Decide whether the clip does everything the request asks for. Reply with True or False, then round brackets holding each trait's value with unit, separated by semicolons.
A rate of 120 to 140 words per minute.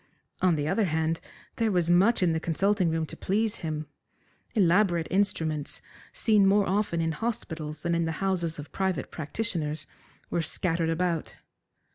False (155 wpm)